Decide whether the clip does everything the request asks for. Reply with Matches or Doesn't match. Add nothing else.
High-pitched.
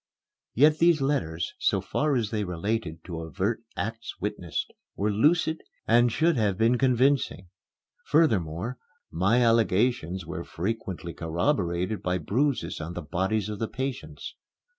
Doesn't match